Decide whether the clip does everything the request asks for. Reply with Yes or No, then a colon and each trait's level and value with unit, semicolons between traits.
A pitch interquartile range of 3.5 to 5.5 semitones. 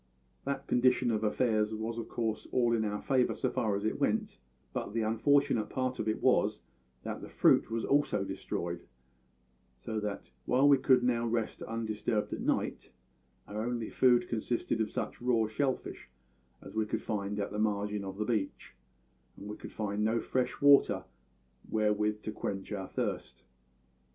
No: narrow, 2.6 semitones